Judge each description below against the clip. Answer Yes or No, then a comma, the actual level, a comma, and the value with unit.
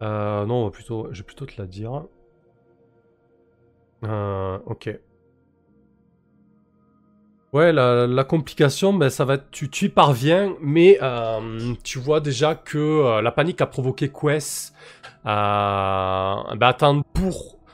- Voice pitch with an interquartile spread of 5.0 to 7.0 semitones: Yes, wide, 5.5 semitones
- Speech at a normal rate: No, slow, 130 wpm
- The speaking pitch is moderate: No, low, 125 Hz